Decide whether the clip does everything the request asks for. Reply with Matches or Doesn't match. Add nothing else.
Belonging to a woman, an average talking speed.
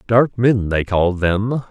Doesn't match